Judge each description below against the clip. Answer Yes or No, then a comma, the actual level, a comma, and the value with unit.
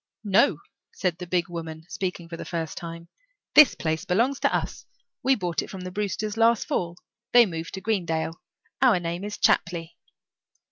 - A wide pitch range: No, average, 3.9 semitones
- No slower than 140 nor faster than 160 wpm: No, average, 175 wpm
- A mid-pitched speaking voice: Yes, medium, 180 Hz